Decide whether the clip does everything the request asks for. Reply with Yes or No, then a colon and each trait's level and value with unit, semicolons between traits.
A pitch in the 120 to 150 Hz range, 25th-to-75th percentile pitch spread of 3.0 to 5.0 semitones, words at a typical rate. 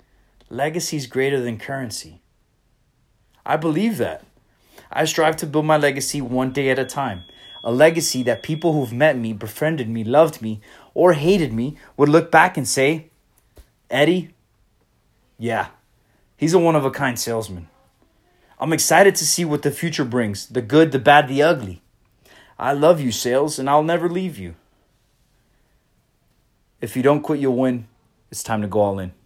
No: low, 135 Hz; wide, 5.4 semitones; average, 170 wpm